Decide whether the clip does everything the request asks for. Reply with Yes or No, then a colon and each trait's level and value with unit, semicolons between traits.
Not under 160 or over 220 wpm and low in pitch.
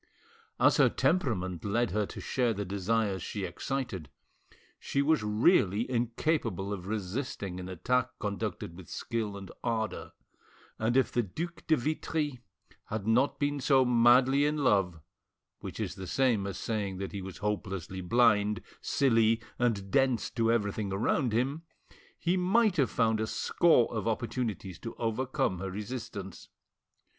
No: average, 150 wpm; low, 115 Hz